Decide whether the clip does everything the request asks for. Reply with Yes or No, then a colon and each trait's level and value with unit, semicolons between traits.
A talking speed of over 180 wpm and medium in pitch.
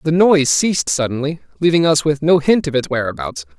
Yes: average, 200 wpm; medium, 145 Hz